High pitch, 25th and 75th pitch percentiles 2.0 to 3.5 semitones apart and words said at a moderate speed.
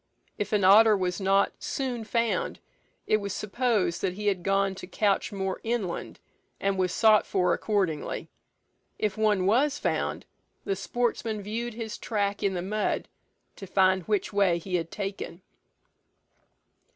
Yes: high, 200 Hz; narrow, 2.4 semitones; average, 150 wpm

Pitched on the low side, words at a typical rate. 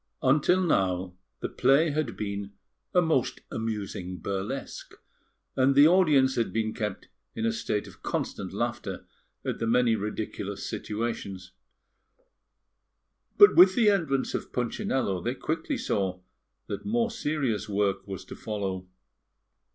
No: low, 115 Hz; slow, 130 wpm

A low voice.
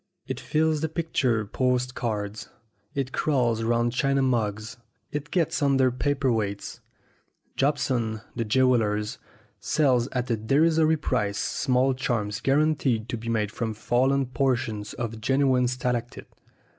Yes: low, 125 Hz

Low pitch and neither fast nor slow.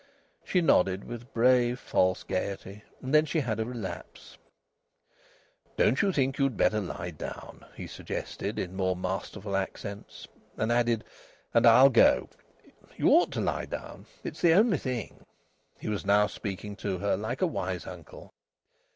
Yes: low, 110 Hz; average, 155 wpm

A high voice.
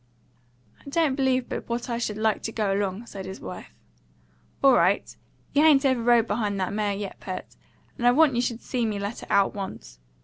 Yes: high, 225 Hz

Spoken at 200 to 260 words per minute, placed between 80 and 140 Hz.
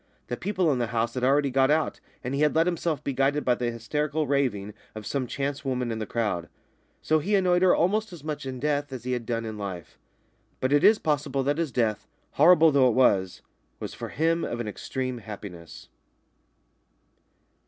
Yes: fast, 205 wpm; low, 135 Hz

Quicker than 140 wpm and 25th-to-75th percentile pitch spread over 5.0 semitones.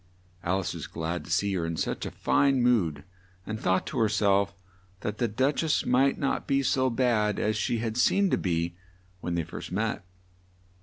Yes: average, 200 wpm; wide, 5.6 semitones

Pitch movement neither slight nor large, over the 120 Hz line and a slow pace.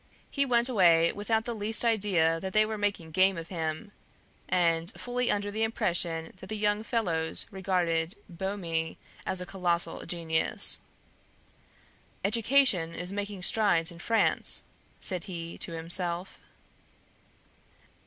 Yes: average, 4.2 semitones; medium, 185 Hz; slow, 130 wpm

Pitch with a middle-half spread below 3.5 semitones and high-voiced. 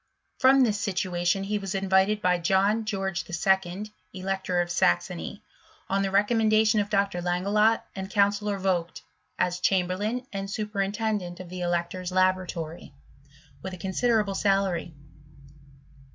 Yes: narrow, 2.5 semitones; high, 195 Hz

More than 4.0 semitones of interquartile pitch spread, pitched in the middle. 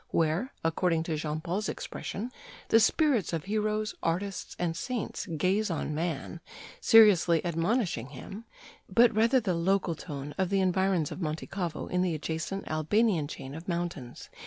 Yes: average, 4.5 semitones; medium, 180 Hz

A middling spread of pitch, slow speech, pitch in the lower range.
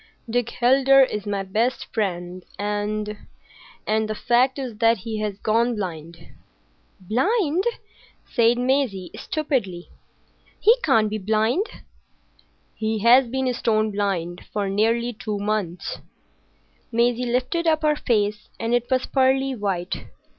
No: average, 3.6 semitones; slow, 120 wpm; high, 225 Hz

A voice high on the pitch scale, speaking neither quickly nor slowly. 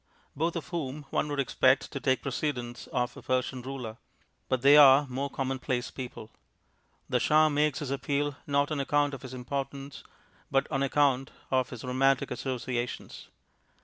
No: low, 135 Hz; average, 160 wpm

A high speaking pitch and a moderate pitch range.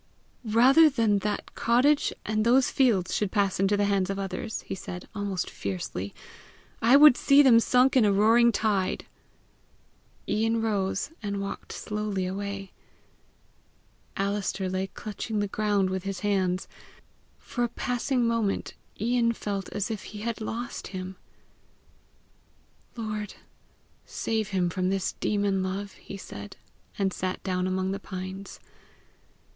Yes: high, 205 Hz; average, 3.0 semitones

